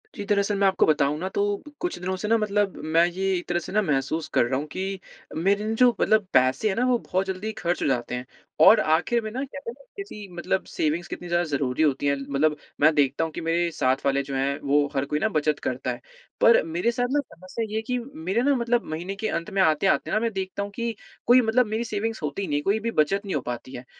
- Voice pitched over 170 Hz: Yes, medium, 185 Hz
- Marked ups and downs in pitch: Yes, wide, 6.4 semitones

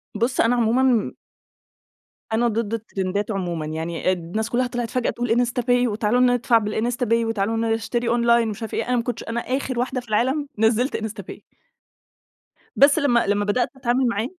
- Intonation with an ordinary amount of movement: No, narrow, 2.3 semitones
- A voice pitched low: No, high, 235 Hz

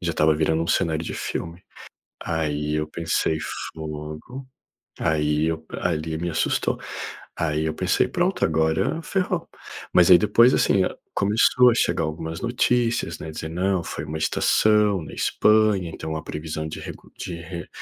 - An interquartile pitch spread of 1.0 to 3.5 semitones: No, average, 4.0 semitones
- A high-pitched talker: No, very low, 80 Hz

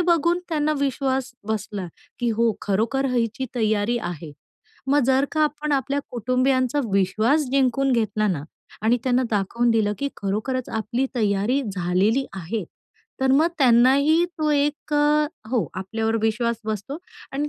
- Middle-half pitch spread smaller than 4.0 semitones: No, average, 4.5 semitones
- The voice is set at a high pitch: Yes, high, 245 Hz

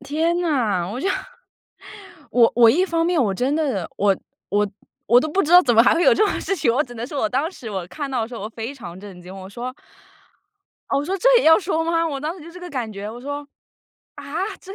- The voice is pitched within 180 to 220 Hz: No, very high, 265 Hz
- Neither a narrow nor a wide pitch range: No, wide, 6.8 semitones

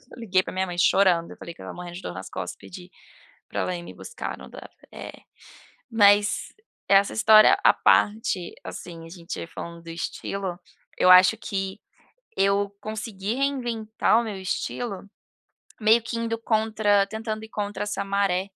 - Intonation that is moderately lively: Yes, average, 3.3 semitones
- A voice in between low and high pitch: No, high, 200 Hz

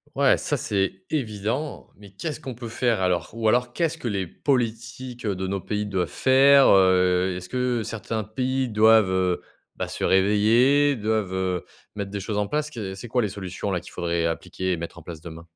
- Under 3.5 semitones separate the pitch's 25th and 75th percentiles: No, average, 4.7 semitones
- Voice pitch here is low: Yes, low, 105 Hz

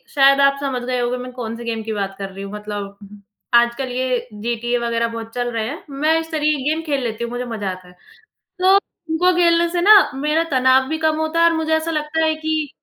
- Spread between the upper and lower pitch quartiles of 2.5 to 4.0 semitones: No, average, 5.3 semitones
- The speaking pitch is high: Yes, very high, 260 Hz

